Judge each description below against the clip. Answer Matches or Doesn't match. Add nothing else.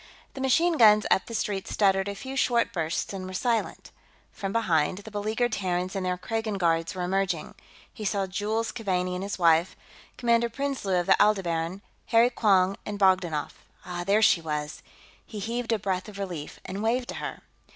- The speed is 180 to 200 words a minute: Matches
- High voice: Matches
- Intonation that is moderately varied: Matches